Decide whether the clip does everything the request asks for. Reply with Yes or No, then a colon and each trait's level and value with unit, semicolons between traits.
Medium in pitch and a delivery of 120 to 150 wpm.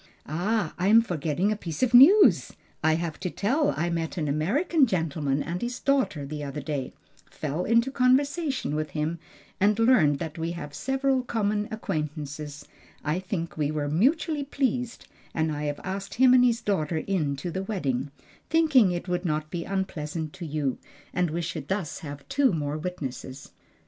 No: medium, 175 Hz; average, 175 wpm